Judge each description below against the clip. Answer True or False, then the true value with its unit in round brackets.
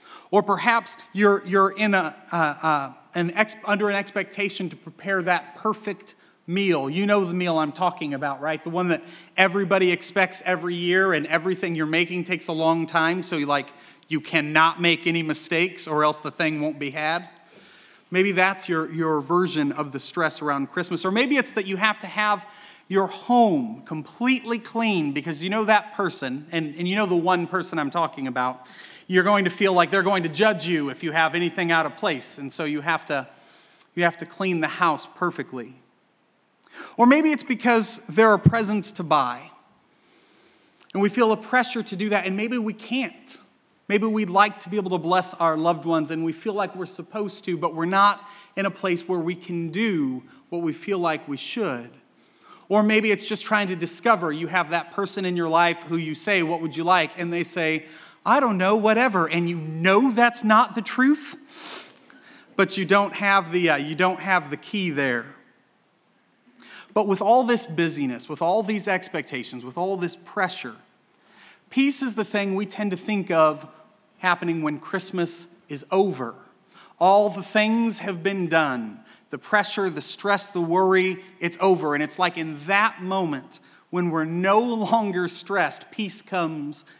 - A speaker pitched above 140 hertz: True (185 Hz)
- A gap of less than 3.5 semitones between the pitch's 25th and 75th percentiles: False (4.0 semitones)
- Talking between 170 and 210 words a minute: True (190 wpm)